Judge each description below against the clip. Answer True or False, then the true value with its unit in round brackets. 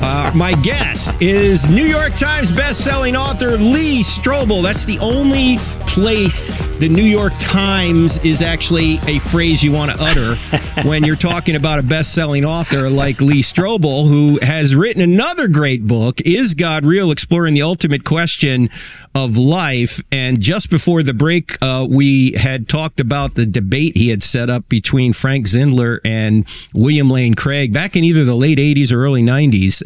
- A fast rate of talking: False (170 wpm)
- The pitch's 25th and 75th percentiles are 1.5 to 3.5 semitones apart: False (4.3 semitones)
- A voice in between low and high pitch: True (145 Hz)